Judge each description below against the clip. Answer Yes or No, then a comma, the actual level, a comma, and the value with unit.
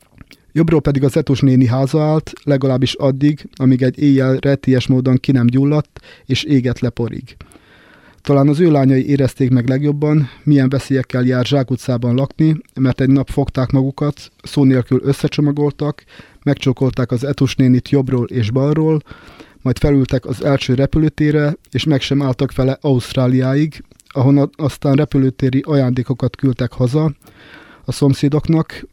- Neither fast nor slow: Yes, average, 135 wpm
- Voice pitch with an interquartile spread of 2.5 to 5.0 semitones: No, narrow, 2.0 semitones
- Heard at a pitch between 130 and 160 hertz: Yes, low, 135 Hz